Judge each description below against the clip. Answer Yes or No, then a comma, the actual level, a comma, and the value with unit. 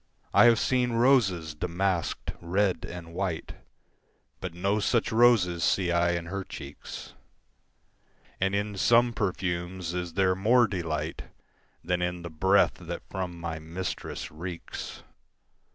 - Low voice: Yes, very low, 90 Hz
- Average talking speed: No, slow, 130 wpm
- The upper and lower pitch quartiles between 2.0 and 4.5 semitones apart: Yes, average, 2.8 semitones